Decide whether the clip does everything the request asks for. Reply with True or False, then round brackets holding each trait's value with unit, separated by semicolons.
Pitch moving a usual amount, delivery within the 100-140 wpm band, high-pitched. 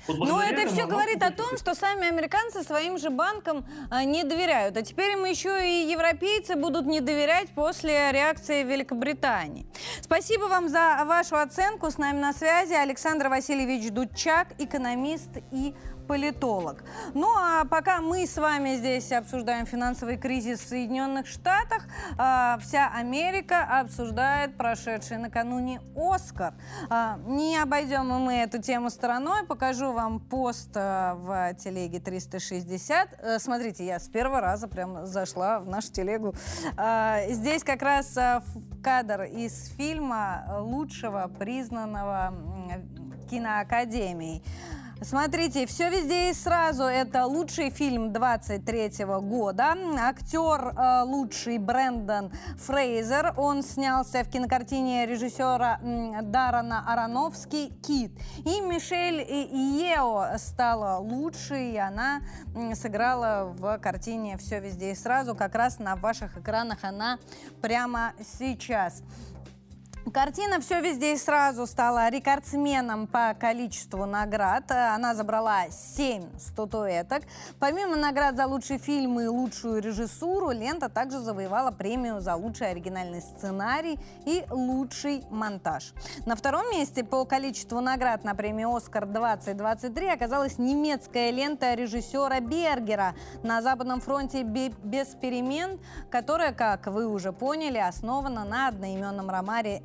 True (4.7 semitones; 120 wpm; 255 Hz)